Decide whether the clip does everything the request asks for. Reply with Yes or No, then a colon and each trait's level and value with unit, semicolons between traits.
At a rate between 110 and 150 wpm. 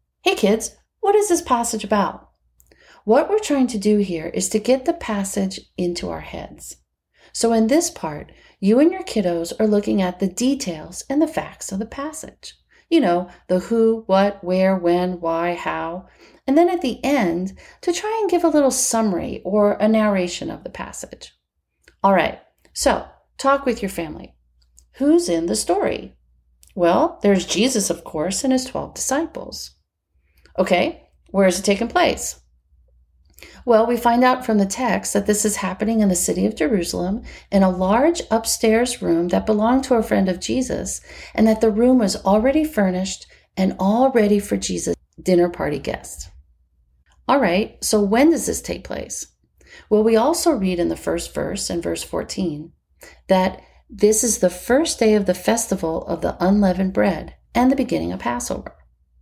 No: average, 175 wpm